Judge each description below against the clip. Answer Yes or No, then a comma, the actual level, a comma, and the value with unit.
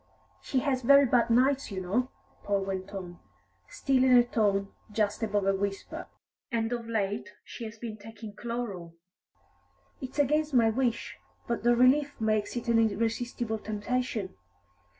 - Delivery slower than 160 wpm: Yes, average, 150 wpm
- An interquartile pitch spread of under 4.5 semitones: Yes, average, 3.4 semitones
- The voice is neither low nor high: No, high, 230 Hz